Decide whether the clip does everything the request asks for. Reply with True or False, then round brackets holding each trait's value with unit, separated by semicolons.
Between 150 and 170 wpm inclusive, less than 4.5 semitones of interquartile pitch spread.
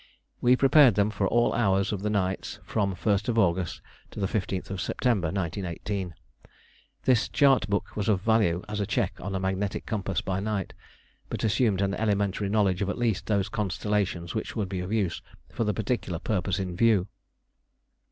False (180 wpm; 2.4 semitones)